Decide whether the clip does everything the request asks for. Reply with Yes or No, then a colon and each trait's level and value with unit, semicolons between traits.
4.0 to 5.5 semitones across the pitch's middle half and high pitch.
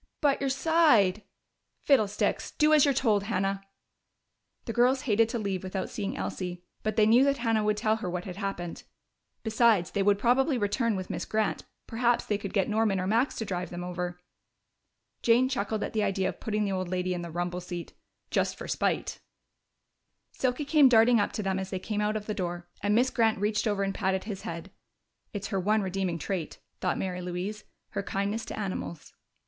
No: average, 3.5 semitones; high, 205 Hz